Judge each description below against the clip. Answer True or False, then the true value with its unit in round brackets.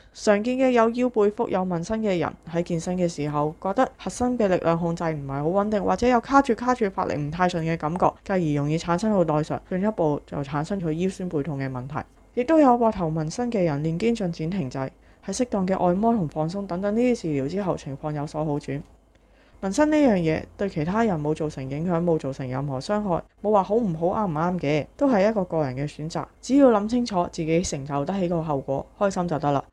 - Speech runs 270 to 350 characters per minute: True (335 characters per minute)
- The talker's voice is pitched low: False (175 Hz)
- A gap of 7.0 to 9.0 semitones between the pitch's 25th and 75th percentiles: False (5.6 semitones)